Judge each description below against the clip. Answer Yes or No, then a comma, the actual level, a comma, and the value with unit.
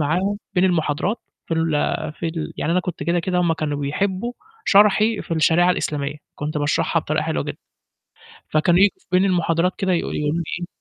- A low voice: No, medium, 170 Hz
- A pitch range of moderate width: Yes, average, 3.3 semitones